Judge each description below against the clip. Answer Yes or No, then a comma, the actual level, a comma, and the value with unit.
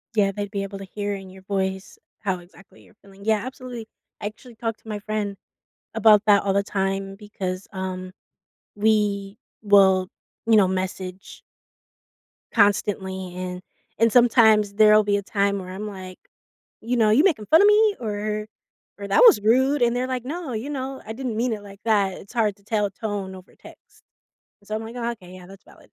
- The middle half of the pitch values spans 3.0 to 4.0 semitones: No, narrow, 2.5 semitones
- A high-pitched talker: Yes, high, 205 Hz